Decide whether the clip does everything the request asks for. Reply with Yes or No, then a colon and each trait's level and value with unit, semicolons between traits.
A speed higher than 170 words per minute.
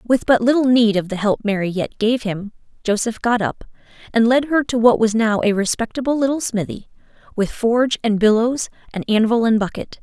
Yes: average, 200 wpm